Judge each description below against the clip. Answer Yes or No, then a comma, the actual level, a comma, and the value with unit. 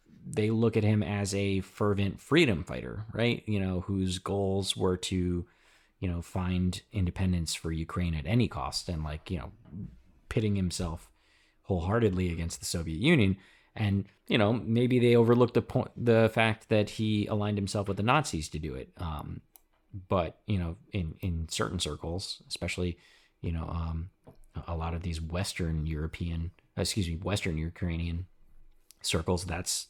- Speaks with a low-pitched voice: Yes, very low, 95 Hz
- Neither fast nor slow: Yes, average, 160 wpm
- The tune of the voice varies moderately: Yes, average, 3.8 semitones